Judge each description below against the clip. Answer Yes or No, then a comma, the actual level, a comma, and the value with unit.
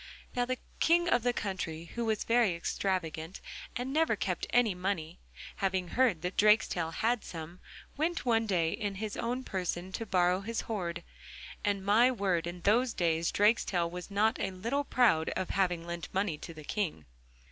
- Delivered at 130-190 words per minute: Yes, average, 175 wpm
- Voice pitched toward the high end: Yes, high, 195 Hz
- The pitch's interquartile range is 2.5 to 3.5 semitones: No, average, 4.8 semitones